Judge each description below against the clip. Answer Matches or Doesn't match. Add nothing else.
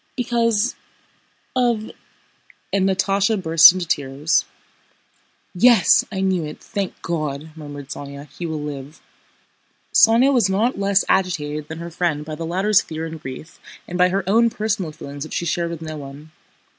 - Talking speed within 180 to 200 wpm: Doesn't match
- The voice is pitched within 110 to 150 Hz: Doesn't match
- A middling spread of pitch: Matches